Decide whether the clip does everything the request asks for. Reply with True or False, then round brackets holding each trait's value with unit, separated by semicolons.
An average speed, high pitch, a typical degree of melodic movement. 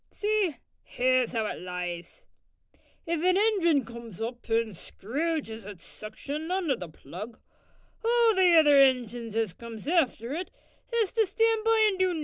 False (160 wpm; 275 Hz; 8.7 semitones)